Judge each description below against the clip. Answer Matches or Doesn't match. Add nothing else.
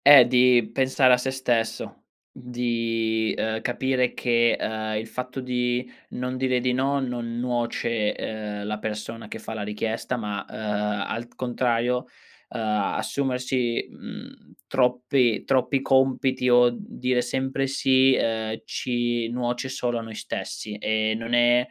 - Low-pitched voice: Matches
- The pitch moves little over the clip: Matches